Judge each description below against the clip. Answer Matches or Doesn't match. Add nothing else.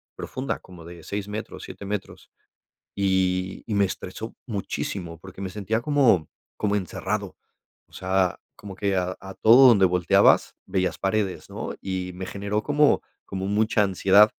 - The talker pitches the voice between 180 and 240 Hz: Doesn't match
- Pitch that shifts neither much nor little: Doesn't match